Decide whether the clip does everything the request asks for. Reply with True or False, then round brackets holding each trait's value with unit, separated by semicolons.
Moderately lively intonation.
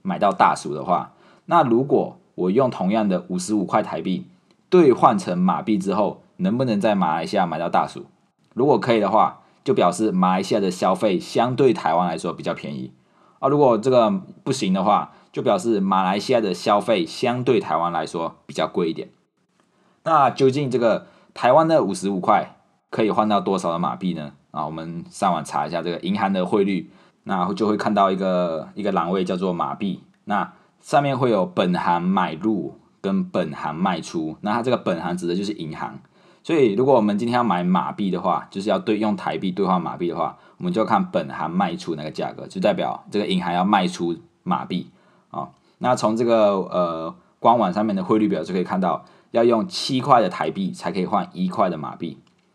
True (3.9 semitones)